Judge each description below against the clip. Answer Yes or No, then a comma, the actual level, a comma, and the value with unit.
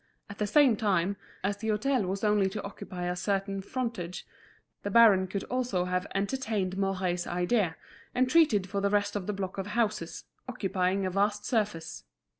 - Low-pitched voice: No, high, 200 Hz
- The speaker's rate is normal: Yes, average, 175 wpm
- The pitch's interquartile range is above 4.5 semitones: No, narrow, 2.4 semitones